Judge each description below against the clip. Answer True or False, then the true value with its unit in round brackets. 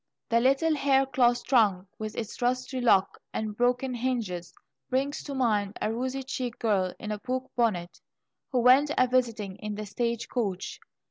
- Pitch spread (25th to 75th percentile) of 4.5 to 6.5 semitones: False (3.4 semitones)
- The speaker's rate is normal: True (170 wpm)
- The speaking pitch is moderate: False (240 Hz)